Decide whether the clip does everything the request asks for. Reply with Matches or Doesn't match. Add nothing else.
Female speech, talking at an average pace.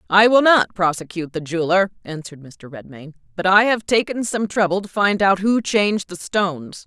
Matches